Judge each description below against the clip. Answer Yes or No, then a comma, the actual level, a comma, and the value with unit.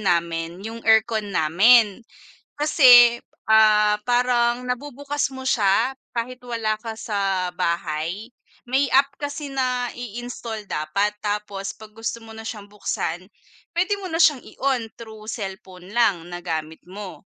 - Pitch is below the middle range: No, high, 220 Hz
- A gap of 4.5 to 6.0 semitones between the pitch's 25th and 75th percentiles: No, average, 4.0 semitones